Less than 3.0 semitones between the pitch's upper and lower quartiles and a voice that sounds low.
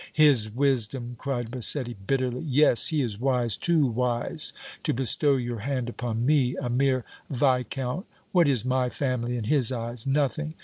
Yes: narrow, 2.5 semitones; low, 125 Hz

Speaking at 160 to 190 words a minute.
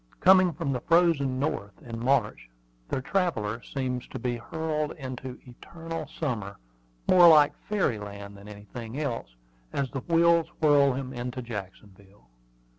No: average, 140 wpm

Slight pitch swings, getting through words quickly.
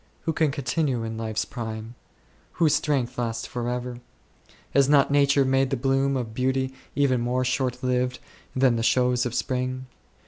No: narrow, 1.9 semitones; average, 160 wpm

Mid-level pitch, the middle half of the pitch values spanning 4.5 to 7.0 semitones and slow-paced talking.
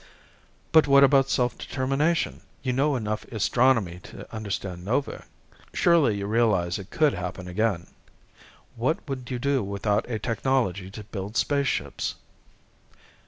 No: low, 115 Hz; average, 5.3 semitones; slow, 130 wpm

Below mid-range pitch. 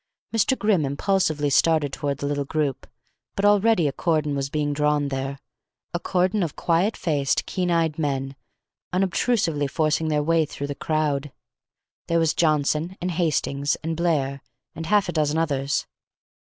No: medium, 155 Hz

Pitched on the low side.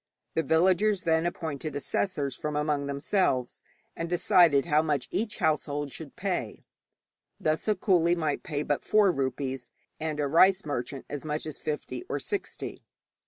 No: medium, 155 Hz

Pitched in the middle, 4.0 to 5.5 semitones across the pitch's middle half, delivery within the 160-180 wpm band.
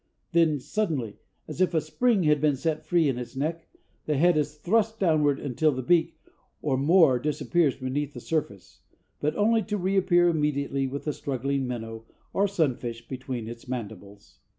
Yes: medium, 150 Hz; average, 4.5 semitones; average, 170 wpm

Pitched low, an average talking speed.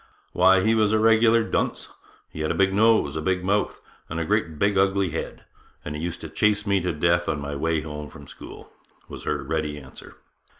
No: very low, 90 Hz; fast, 215 wpm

